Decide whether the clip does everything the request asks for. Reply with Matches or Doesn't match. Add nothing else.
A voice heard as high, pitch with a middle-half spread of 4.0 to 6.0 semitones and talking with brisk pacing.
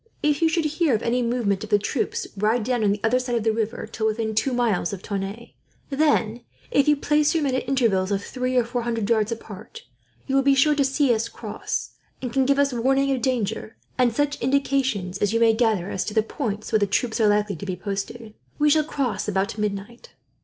Matches